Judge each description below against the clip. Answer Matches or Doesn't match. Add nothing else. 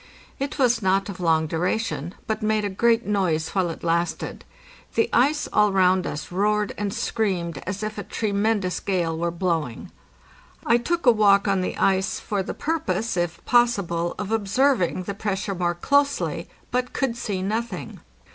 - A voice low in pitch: Doesn't match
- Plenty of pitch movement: Doesn't match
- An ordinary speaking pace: Matches